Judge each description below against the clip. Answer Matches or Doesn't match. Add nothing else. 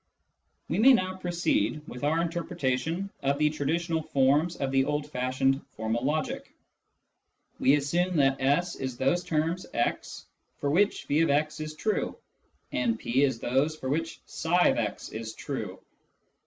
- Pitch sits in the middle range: Matches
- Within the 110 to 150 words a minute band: Matches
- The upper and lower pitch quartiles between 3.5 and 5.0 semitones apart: Matches